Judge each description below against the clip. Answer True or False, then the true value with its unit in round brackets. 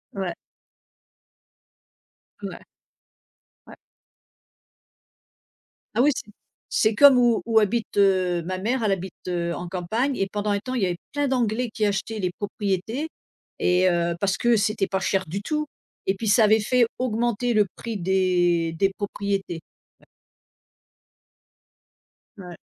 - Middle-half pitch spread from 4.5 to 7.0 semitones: False (3.7 semitones)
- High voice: True (205 Hz)